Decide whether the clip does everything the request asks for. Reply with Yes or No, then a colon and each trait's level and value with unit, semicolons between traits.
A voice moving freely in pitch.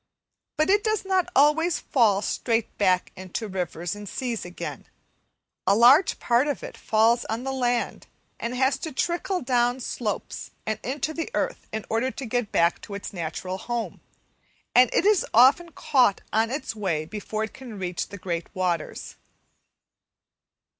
No: average, 5.0 semitones